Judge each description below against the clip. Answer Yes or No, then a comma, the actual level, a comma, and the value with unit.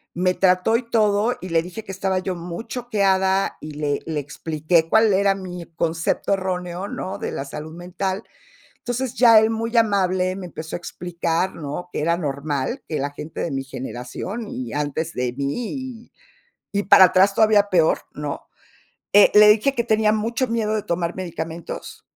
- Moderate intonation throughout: Yes, average, 4.6 semitones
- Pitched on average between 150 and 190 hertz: Yes, medium, 185 Hz